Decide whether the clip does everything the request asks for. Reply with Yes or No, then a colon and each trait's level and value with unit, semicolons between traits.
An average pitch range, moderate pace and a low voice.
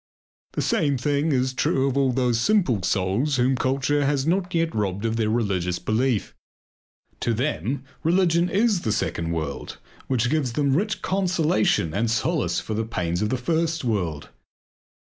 No: wide, 6.0 semitones; average, 160 wpm; low, 130 Hz